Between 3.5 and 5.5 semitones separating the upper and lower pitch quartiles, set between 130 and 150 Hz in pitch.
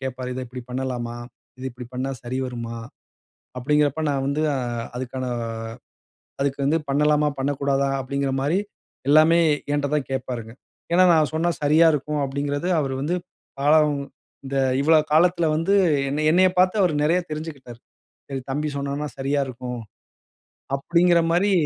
No: average, 2.8 semitones; medium, 140 Hz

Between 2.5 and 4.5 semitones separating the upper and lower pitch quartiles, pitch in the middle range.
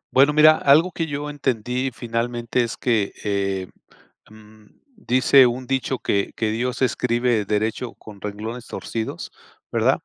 No: average, 3.2 semitones; low, 120 Hz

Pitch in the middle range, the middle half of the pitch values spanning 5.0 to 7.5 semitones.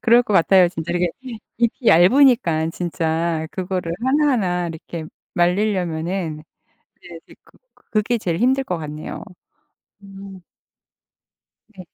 No: medium, 180 Hz; average, 4.5 semitones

